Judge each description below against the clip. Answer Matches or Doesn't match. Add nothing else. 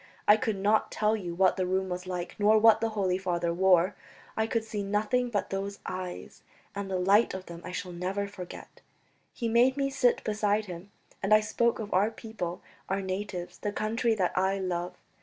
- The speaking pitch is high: Matches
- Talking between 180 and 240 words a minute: Matches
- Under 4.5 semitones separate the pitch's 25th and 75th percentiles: Matches